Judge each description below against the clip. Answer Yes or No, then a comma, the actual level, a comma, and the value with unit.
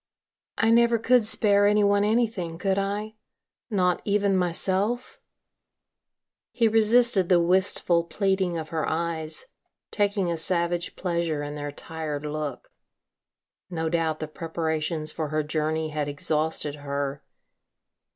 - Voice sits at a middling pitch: Yes, medium, 170 Hz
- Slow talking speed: Yes, slow, 125 wpm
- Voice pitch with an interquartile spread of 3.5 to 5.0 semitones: Yes, average, 4.5 semitones